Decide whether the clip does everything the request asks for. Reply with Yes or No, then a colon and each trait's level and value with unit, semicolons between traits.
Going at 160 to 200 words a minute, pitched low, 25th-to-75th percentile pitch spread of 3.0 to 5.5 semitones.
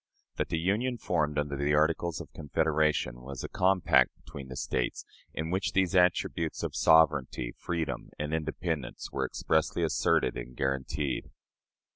No: average, 145 wpm; very low, 75 Hz; average, 3.4 semitones